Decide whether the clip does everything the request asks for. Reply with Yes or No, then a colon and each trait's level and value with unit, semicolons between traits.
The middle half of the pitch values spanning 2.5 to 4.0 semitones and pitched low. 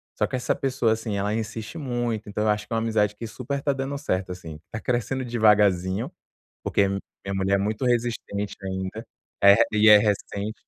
Yes: average, 3.2 semitones; low, 110 Hz